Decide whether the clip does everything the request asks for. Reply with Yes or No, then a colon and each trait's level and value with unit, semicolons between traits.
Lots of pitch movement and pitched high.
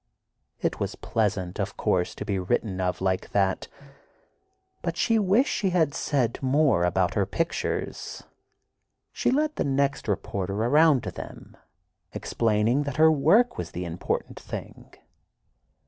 No: wide, 8.7 semitones; low, 120 Hz